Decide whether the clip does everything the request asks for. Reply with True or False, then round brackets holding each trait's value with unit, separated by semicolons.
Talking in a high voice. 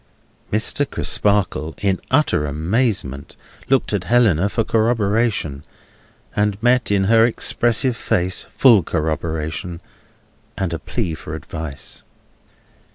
False (100 Hz)